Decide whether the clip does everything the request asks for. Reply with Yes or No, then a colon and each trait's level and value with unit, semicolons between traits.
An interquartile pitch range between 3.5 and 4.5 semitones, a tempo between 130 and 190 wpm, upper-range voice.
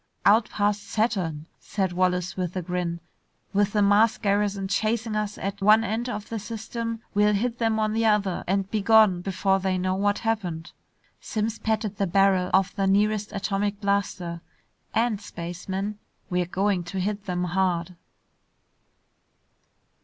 No: narrow, 2.5 semitones; average, 155 wpm; high, 200 Hz